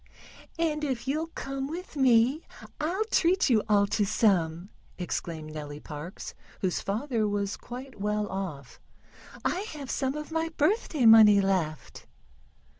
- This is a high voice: Yes, high, 225 Hz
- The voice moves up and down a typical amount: No, wide, 7.6 semitones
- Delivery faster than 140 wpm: No, slow, 135 wpm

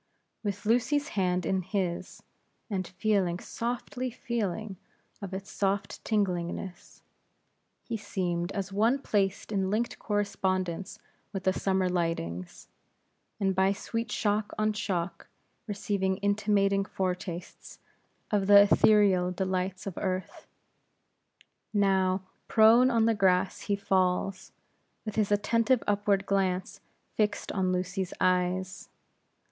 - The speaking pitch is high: Yes, high, 195 Hz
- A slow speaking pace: Yes, slow, 115 wpm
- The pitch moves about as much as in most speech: No, narrow, 2.0 semitones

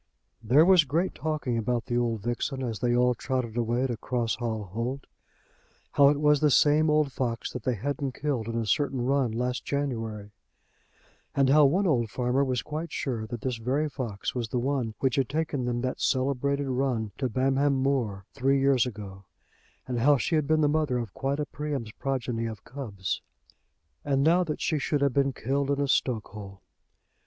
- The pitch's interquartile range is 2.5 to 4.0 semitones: Yes, average, 3.3 semitones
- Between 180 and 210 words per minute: Yes, average, 190 wpm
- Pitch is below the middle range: Yes, low, 130 Hz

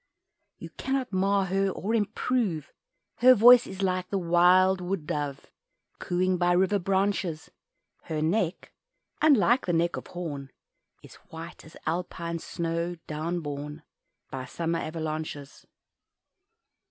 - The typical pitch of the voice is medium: Yes, medium, 175 Hz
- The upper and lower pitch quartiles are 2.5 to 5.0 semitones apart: Yes, average, 3.4 semitones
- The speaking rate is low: Yes, slow, 125 wpm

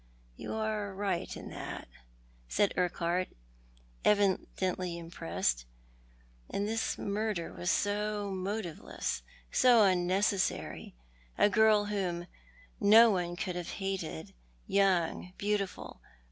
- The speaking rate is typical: No, slow, 105 wpm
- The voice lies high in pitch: Yes, high, 195 Hz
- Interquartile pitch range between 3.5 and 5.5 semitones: No, average, 2.9 semitones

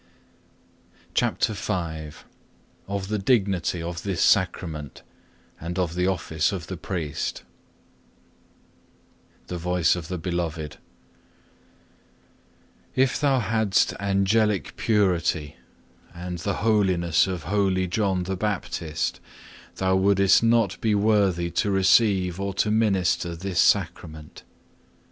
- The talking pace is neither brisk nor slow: No, slow, 110 wpm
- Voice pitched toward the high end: No, very low, 95 Hz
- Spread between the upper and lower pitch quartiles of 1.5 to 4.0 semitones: Yes, average, 2.9 semitones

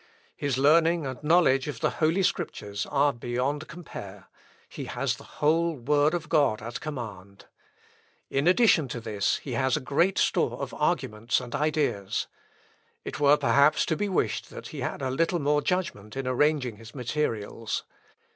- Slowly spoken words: No, average, 160 wpm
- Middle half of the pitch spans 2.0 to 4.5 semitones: No, average, 4.9 semitones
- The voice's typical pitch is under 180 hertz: Yes, medium, 140 Hz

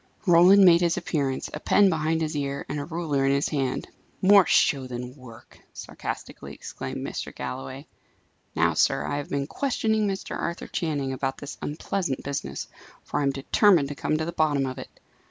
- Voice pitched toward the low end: No, medium, 145 Hz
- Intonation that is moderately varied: Yes, average, 4.0 semitones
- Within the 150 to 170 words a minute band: No, average, 185 wpm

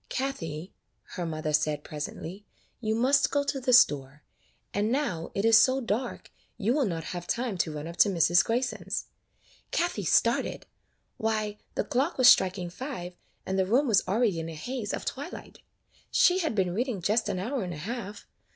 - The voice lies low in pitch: No, high, 210 Hz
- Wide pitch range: Yes, wide, 6.4 semitones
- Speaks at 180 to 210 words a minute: Yes, average, 185 wpm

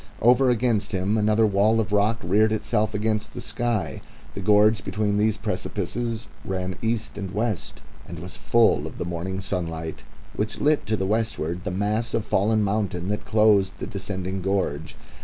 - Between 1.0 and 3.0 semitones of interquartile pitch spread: Yes, narrow, 2.5 semitones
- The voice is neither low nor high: No, low, 105 Hz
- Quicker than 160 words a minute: Yes, average, 170 wpm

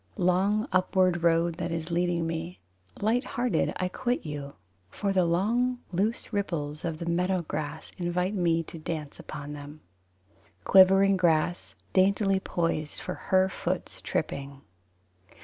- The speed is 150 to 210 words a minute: No, slow, 135 wpm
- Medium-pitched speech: Yes, medium, 175 Hz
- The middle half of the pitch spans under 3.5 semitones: Yes, average, 3.0 semitones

